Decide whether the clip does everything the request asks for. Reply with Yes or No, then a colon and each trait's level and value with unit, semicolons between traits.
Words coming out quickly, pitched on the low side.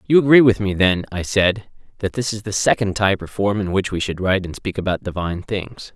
Yes: fast, 250 wpm; low, 100 Hz